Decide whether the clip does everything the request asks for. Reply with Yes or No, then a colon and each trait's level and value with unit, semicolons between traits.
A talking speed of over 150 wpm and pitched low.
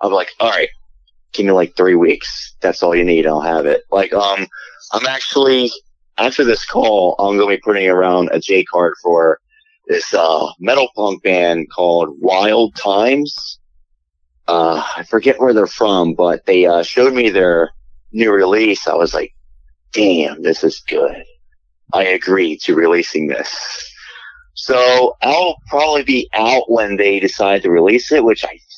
Yes: average, 165 wpm; low, 100 Hz